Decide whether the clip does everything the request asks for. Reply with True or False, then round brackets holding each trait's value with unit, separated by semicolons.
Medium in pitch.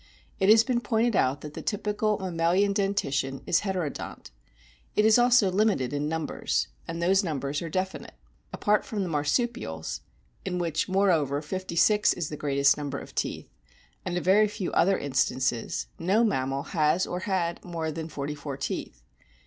True (170 Hz)